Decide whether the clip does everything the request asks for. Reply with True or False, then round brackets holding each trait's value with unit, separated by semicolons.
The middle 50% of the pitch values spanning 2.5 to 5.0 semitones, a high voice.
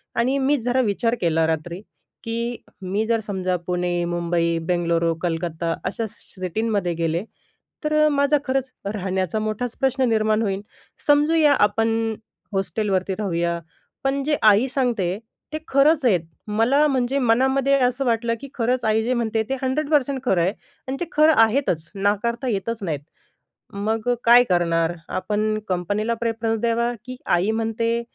False (5.4 semitones; 220 Hz)